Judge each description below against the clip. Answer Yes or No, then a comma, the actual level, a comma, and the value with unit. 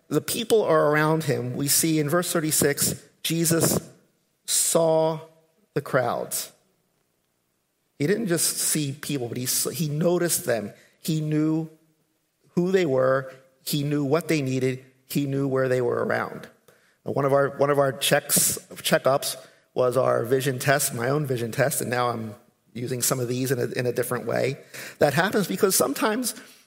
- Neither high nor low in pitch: Yes, medium, 150 Hz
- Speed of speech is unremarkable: Yes, average, 165 wpm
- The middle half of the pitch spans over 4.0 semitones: No, average, 3.7 semitones